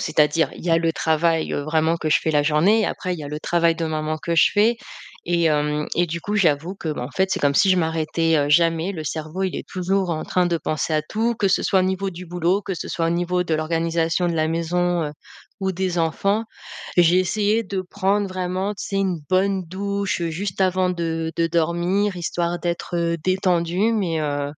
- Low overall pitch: No, medium, 170 Hz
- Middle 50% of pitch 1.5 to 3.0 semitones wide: Yes, narrow, 2.6 semitones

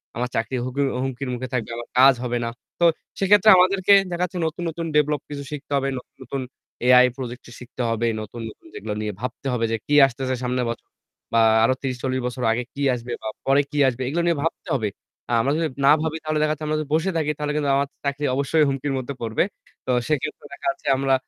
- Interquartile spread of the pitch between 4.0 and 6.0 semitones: No, average, 3.5 semitones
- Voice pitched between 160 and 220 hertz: No, low, 135 Hz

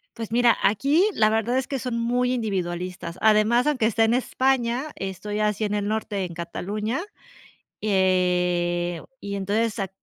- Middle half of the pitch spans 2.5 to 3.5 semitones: No, average, 3.9 semitones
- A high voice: Yes, high, 215 Hz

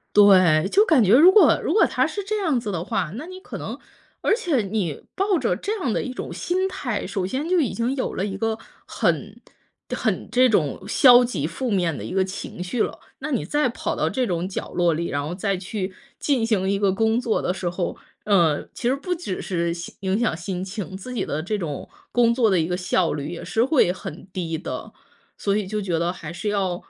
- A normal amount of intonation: No, wide, 6.0 semitones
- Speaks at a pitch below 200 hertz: No, high, 205 Hz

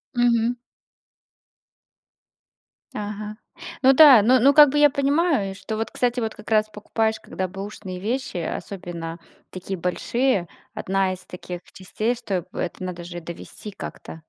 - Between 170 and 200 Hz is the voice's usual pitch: No, high, 210 Hz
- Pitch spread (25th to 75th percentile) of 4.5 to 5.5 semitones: Yes, average, 4.8 semitones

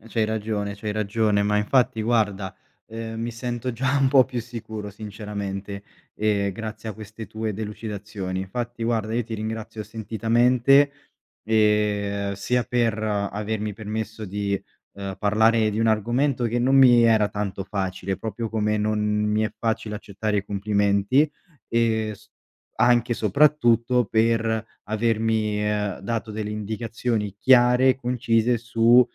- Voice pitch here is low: Yes, low, 110 Hz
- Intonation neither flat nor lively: No, narrow, 2.0 semitones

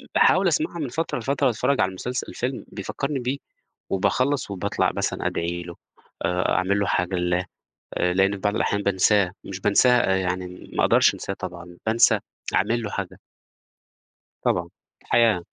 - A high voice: No, low, 100 Hz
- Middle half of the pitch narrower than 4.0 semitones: No, average, 5.3 semitones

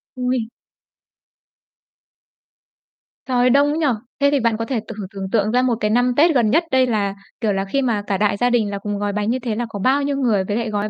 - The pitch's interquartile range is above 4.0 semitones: No, average, 3.7 semitones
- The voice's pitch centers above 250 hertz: No, high, 230 Hz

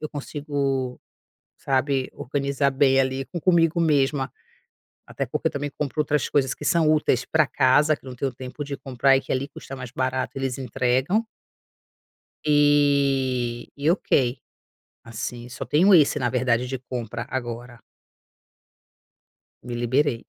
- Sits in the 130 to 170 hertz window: Yes, low, 135 Hz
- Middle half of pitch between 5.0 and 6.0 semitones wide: No, narrow, 2.5 semitones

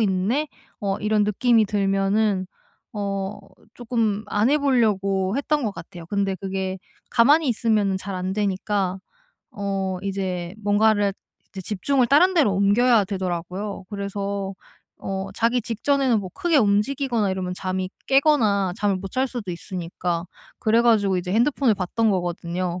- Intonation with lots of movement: No, average, 3.3 semitones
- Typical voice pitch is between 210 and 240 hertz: No, high, 200 Hz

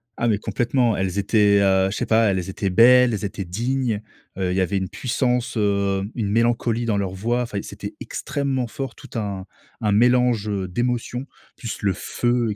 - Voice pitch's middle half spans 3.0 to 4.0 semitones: Yes, average, 3.7 semitones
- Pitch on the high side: No, low, 110 Hz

